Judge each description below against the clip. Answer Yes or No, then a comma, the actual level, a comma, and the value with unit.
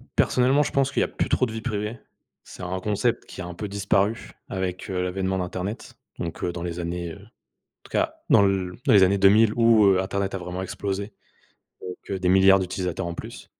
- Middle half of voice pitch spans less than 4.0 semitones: Yes, narrow, 2.6 semitones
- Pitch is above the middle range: No, very low, 95 Hz